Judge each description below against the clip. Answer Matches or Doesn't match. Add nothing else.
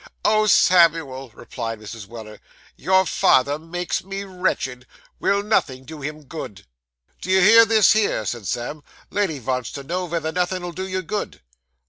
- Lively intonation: Matches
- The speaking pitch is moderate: Matches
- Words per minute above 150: Matches